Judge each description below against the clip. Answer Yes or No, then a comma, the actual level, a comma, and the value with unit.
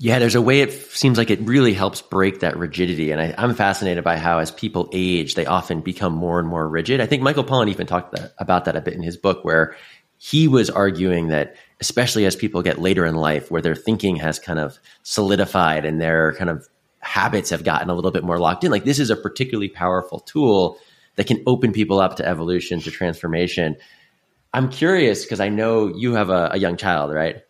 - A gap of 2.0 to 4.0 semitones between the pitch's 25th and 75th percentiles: No, average, 4.9 semitones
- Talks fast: Yes, fast, 225 wpm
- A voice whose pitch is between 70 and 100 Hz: Yes, very low, 90 Hz